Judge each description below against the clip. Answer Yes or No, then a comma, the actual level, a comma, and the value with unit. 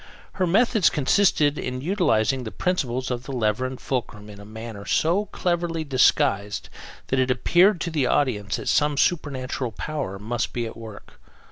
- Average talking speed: Yes, average, 165 wpm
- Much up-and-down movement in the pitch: Yes, wide, 6.4 semitones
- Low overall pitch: Yes, low, 130 Hz